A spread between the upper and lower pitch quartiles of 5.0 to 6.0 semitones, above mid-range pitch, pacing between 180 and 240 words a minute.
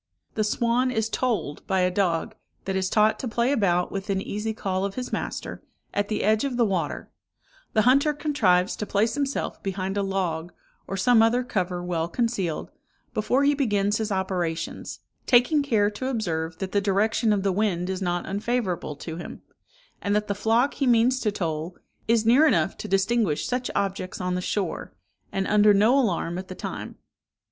No: average, 4.1 semitones; high, 205 Hz; average, 185 wpm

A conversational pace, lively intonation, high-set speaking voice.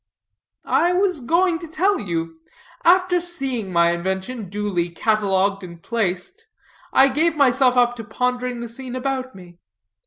Yes: average, 145 wpm; wide, 7.0 semitones; high, 245 Hz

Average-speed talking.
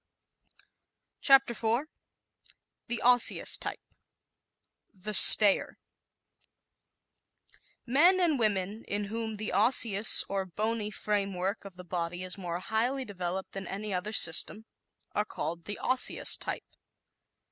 No: slow, 115 wpm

